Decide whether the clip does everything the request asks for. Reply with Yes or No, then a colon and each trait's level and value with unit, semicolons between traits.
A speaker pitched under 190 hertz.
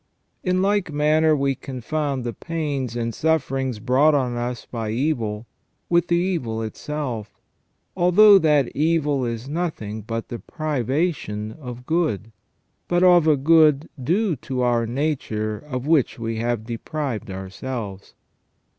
Yes: low, 135 Hz